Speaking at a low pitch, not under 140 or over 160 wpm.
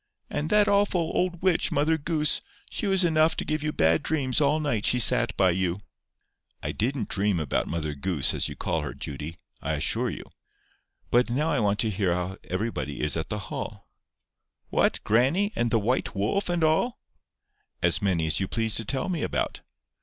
No: low, 120 Hz; average, 190 wpm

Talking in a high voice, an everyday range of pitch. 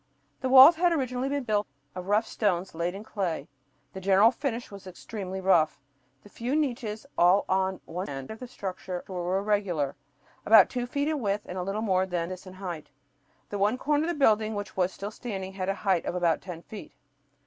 Yes: high, 200 Hz; average, 3.9 semitones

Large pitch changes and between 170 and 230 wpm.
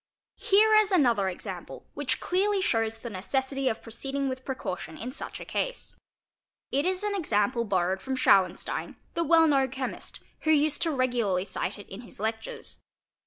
Yes: wide, 6.3 semitones; average, 180 wpm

